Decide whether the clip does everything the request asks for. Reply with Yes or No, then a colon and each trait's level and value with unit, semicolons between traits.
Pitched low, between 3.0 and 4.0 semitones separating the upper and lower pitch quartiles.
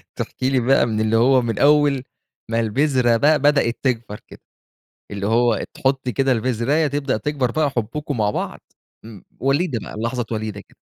Yes: low, 125 Hz; average, 3.7 semitones